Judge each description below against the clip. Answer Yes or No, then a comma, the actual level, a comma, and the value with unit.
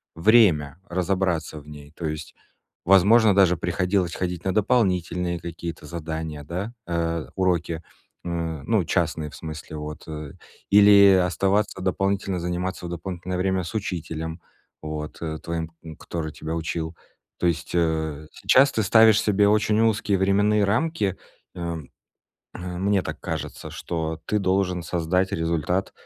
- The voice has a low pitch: Yes, very low, 90 Hz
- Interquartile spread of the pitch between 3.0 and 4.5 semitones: Yes, average, 3.3 semitones